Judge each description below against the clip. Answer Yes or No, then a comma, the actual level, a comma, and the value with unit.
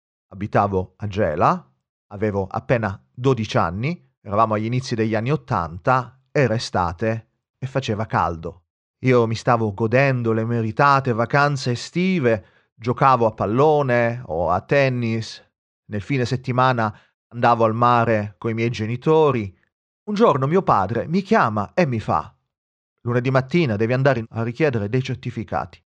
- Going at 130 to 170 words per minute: Yes, average, 135 wpm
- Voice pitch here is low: Yes, low, 120 Hz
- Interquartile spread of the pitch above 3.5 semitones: No, average, 3.2 semitones